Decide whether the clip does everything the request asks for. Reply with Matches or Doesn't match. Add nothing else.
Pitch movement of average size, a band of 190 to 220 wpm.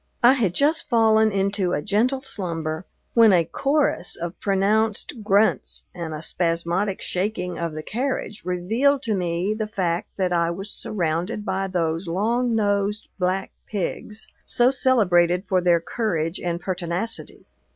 Doesn't match